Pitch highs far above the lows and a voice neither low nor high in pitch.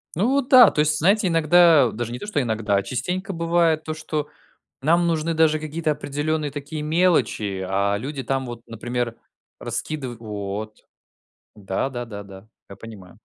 Yes: wide, 6.4 semitones; medium, 145 Hz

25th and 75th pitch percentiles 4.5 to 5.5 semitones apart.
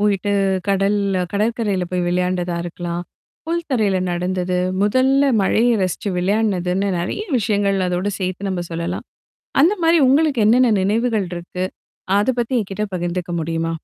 No: average, 3.7 semitones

